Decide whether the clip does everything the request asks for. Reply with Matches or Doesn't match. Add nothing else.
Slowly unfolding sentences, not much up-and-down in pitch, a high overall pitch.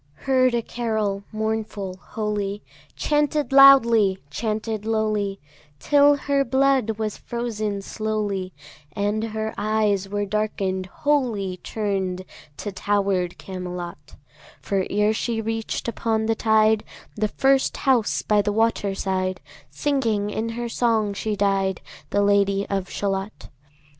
Matches